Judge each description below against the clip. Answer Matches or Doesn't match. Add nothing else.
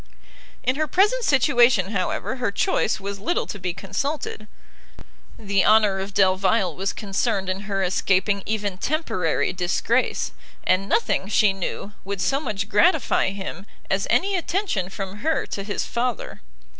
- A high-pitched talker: Matches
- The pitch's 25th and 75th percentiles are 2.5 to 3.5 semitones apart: Doesn't match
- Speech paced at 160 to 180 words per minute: Doesn't match